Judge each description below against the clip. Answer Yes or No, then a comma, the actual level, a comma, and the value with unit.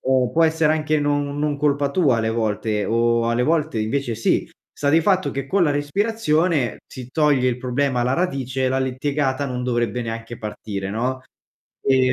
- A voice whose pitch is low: Yes, low, 130 Hz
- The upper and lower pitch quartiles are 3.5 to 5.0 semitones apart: Yes, average, 3.9 semitones